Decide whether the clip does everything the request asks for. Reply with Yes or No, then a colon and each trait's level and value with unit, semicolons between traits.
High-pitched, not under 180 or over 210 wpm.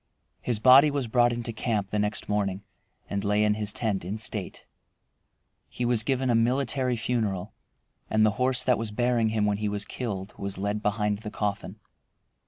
No: low, 110 Hz; average, 185 wpm